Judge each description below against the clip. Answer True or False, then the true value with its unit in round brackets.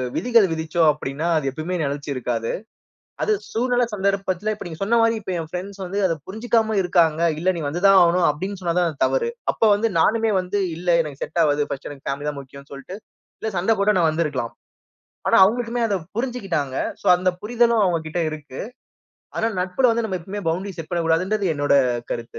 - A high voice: False (180 Hz)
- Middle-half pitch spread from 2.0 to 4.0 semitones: False (5.3 semitones)